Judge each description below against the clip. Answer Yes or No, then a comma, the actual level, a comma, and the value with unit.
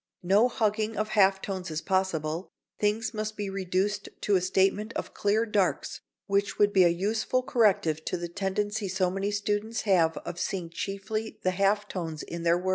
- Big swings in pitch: No, narrow, 2.4 semitones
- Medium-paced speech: Yes, average, 185 wpm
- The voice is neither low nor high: No, high, 195 Hz